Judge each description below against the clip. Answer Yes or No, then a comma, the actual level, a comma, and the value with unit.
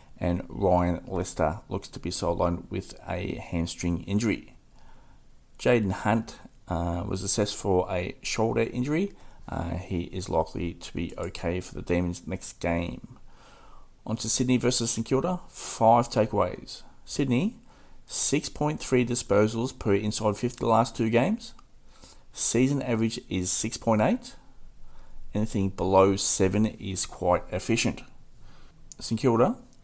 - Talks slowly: Yes, slow, 125 wpm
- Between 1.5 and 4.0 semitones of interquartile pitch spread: No, average, 4.5 semitones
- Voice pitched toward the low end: Yes, low, 105 Hz